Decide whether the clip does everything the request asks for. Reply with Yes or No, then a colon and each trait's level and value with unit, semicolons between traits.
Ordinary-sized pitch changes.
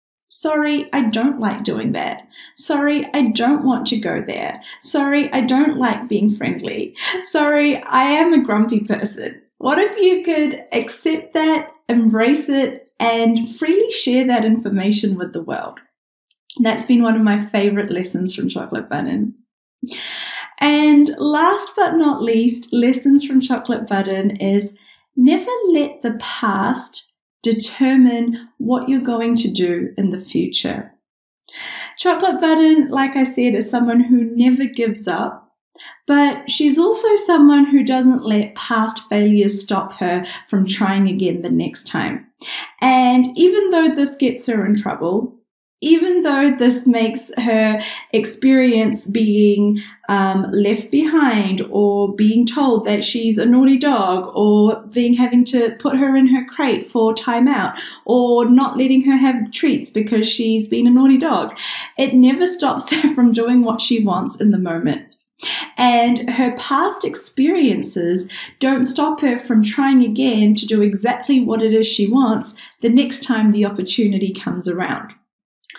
Yes: average, 4.4 semitones